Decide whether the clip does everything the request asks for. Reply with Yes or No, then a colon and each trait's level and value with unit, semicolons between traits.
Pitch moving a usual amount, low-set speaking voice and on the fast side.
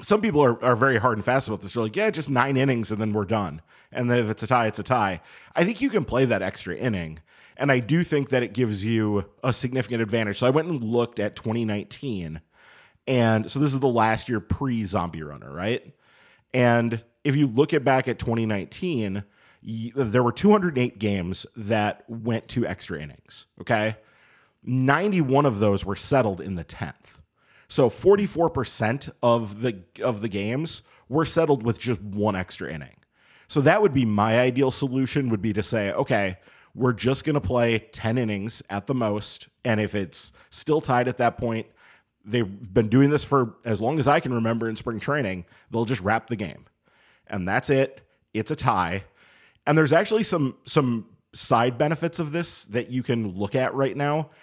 No: average, 4.0 semitones; low, 120 Hz; average, 195 wpm